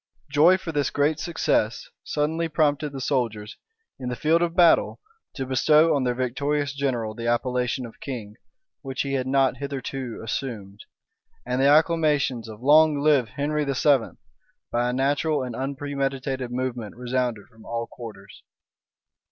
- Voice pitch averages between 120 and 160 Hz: Yes, low, 135 Hz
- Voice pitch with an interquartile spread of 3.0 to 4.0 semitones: Yes, average, 3.3 semitones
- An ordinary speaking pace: Yes, average, 150 wpm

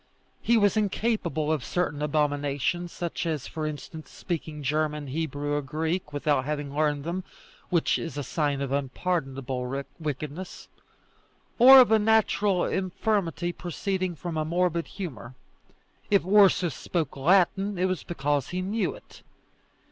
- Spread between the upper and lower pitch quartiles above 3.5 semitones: Yes, average, 4.2 semitones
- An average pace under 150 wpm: Yes, average, 140 wpm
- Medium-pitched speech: Yes, medium, 160 Hz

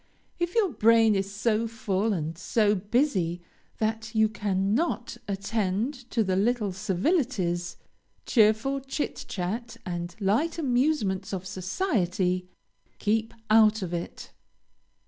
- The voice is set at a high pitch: Yes, high, 215 Hz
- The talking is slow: Yes, slow, 115 wpm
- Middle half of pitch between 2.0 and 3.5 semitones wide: No, average, 3.9 semitones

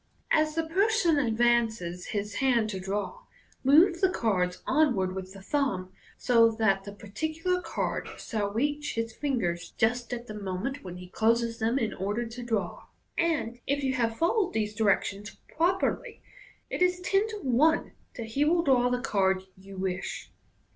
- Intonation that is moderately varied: No, wide, 6.6 semitones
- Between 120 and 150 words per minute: No, average, 170 wpm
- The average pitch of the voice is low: No, high, 235 Hz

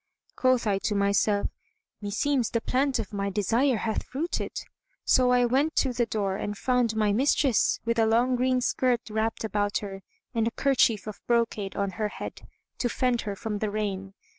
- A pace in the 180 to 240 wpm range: Yes, average, 185 wpm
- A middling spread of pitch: Yes, average, 3.4 semitones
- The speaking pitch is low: No, high, 225 Hz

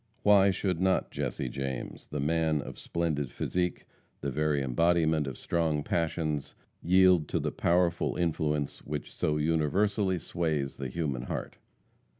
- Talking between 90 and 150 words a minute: Yes, average, 140 wpm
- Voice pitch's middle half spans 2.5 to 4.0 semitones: Yes, average, 3.1 semitones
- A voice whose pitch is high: No, very low, 80 Hz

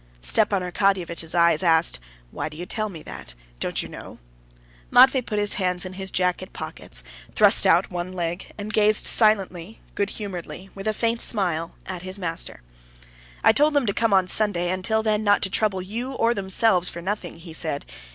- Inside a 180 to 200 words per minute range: Yes, average, 190 wpm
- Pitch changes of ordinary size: Yes, average, 3.4 semitones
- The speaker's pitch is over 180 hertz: Yes, high, 190 Hz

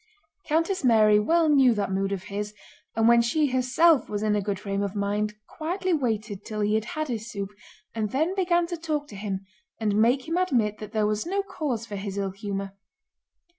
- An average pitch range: No, wide, 6.8 semitones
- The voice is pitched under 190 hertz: No, high, 220 Hz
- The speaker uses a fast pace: Yes, fast, 210 wpm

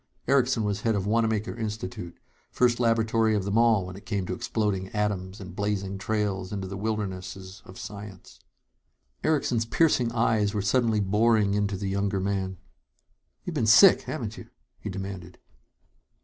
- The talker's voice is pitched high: No, low, 105 Hz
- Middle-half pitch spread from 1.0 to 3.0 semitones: Yes, average, 2.7 semitones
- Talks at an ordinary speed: Yes, average, 155 wpm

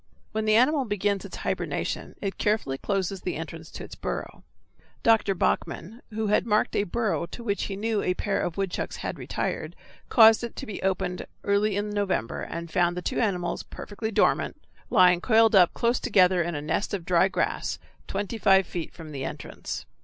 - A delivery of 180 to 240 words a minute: Yes, average, 190 wpm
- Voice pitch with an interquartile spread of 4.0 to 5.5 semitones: No, average, 3.4 semitones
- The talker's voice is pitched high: Yes, high, 195 Hz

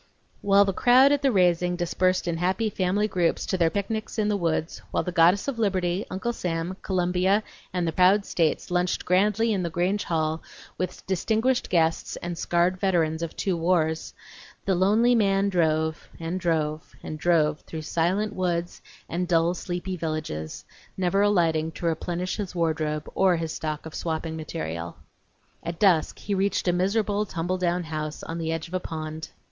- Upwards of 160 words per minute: Yes, average, 175 wpm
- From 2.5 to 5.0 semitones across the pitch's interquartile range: Yes, average, 3.0 semitones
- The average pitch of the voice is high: No, medium, 175 Hz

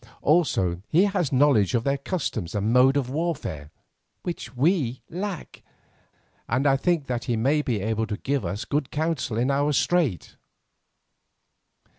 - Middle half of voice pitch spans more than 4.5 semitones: Yes, average, 5.2 semitones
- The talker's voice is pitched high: No, low, 135 Hz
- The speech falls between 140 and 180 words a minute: Yes, average, 150 wpm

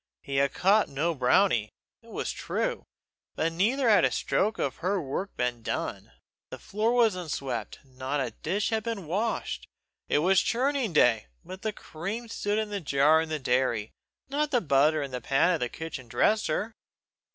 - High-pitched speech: No, medium, 170 Hz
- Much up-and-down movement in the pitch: Yes, wide, 7.6 semitones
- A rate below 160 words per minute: No, average, 180 wpm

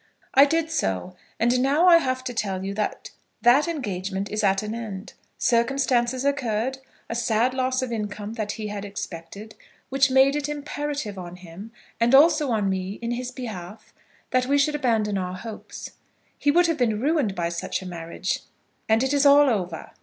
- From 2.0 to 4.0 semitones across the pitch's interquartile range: No, average, 5.2 semitones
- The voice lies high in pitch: Yes, high, 235 Hz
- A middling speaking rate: Yes, average, 185 wpm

